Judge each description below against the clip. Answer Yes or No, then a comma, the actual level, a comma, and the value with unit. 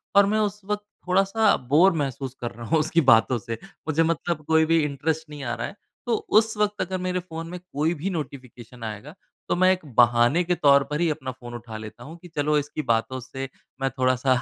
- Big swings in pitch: Yes, wide, 5.7 semitones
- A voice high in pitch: No, medium, 150 Hz